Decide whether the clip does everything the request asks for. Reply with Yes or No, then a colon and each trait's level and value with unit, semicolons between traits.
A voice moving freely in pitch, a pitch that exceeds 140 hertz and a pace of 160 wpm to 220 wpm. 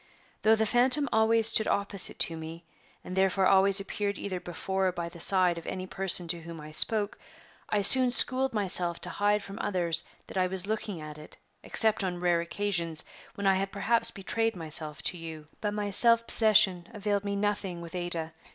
No: average, 3.3 semitones; high, 190 Hz; average, 195 wpm